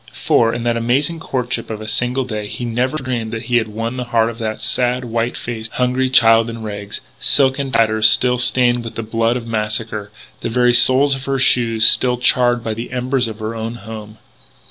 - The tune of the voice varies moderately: No, narrow, 2.0 semitones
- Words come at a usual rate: No, fast, 210 wpm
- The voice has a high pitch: No, low, 115 Hz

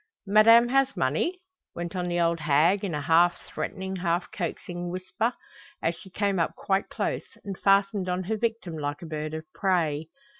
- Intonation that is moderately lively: Yes, average, 3.2 semitones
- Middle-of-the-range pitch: Yes, medium, 180 Hz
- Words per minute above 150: Yes, average, 180 wpm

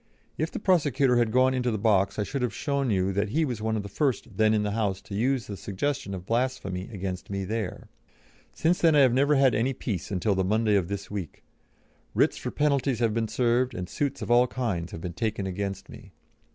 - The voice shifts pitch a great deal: No, average, 4.7 semitones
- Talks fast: Yes, fast, 230 wpm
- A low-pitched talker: Yes, low, 110 Hz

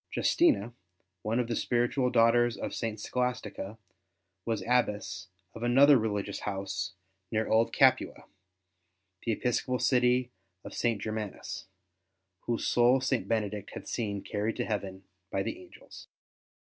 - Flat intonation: No, average, 3.1 semitones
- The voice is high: No, low, 115 Hz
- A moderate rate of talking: No, slow, 130 wpm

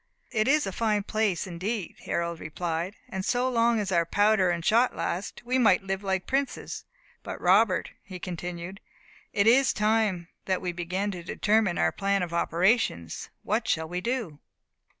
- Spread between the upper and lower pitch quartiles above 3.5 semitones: Yes, average, 4.0 semitones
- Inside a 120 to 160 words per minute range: No, average, 170 wpm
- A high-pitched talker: Yes, high, 195 Hz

